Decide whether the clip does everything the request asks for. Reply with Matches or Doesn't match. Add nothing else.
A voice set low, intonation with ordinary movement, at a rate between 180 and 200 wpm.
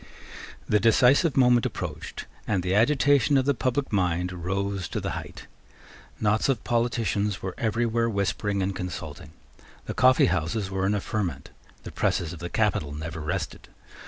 Doesn't match